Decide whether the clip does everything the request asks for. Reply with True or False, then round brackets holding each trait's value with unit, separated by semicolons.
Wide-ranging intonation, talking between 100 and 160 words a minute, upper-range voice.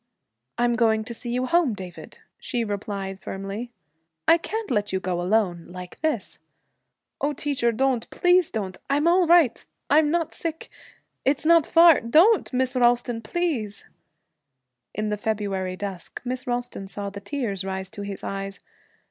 True (6.6 semitones; 155 wpm; 235 Hz)